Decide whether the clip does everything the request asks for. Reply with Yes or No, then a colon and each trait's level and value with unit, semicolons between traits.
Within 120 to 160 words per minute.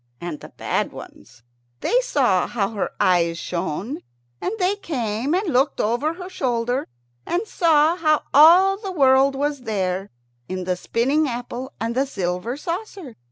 Yes: average, 155 wpm